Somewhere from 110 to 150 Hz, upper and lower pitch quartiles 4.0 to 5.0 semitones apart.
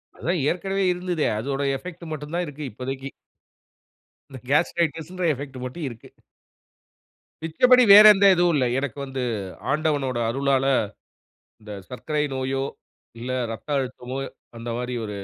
Yes: medium, 140 Hz; average, 4.6 semitones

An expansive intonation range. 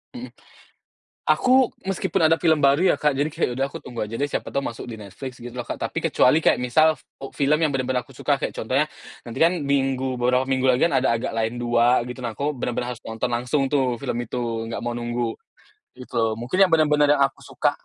No: average, 3.5 semitones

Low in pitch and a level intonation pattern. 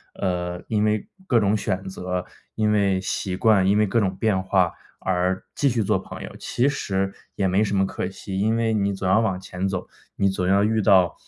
Yes: very low, 95 Hz; narrow, 2.2 semitones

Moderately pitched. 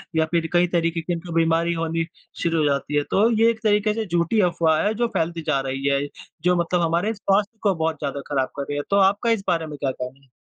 Yes: medium, 165 Hz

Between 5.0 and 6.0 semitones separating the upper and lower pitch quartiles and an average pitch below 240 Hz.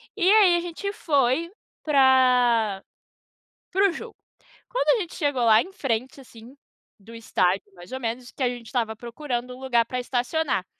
No: wide, 5.4 semitones; very high, 255 Hz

